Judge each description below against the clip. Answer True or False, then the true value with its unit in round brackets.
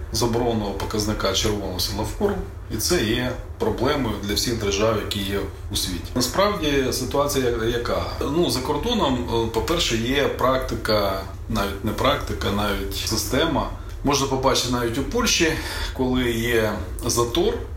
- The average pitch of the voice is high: False (110 Hz)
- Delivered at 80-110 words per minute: False (130 wpm)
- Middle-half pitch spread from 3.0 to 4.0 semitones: True (3.7 semitones)